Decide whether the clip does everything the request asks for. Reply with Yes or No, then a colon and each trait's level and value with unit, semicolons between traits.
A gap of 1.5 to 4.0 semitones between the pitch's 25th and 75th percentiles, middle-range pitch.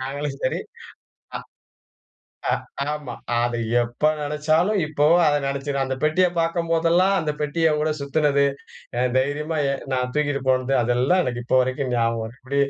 Yes: average, 3.3 semitones; medium, 145 Hz